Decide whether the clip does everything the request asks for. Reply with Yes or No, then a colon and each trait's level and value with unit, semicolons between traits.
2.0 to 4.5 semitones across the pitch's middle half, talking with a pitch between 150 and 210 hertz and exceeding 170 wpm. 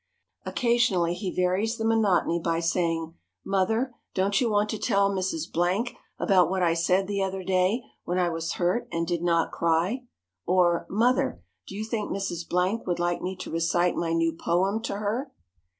Yes: average, 3.3 semitones; medium, 185 Hz; average, 180 wpm